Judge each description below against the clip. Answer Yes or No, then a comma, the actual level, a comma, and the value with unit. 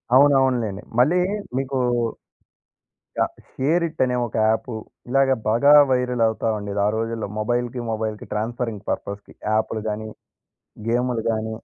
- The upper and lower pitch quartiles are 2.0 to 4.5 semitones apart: Yes, average, 2.9 semitones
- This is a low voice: Yes, low, 115 Hz